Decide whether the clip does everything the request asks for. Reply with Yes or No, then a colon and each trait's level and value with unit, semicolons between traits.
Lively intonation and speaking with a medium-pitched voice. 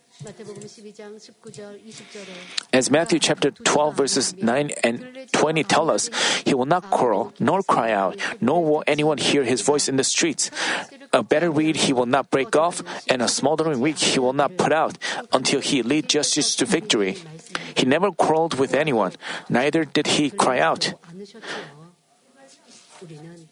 Yes: wide, 6.0 semitones; medium, 160 Hz